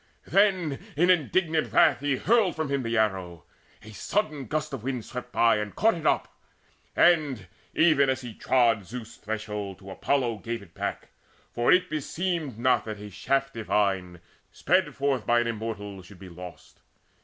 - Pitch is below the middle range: Yes, low, 120 Hz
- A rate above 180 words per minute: No, average, 170 wpm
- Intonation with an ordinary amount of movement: No, wide, 6.4 semitones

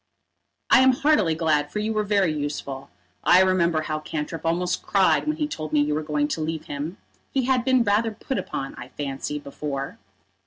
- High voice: No, medium, 165 Hz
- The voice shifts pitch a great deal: Yes, wide, 6.1 semitones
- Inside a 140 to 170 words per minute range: No, average, 195 wpm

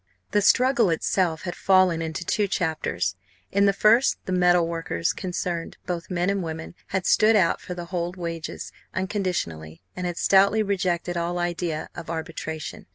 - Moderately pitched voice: Yes, medium, 175 Hz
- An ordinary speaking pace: Yes, average, 160 wpm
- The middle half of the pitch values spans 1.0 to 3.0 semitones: Yes, narrow, 2.5 semitones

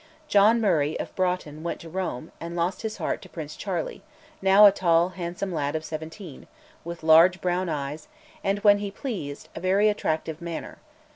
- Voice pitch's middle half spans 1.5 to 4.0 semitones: Yes, average, 3.6 semitones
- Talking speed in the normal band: Yes, average, 180 wpm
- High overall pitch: No, medium, 175 Hz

